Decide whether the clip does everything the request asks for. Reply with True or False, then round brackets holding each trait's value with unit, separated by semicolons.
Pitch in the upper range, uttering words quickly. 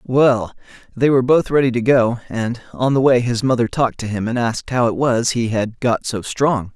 False (120 Hz; 230 wpm)